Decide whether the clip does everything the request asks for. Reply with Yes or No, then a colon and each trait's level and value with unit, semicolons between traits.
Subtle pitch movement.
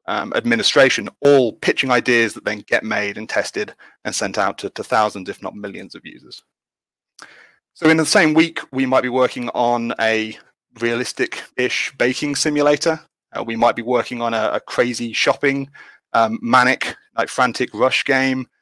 No: average, 3.2 semitones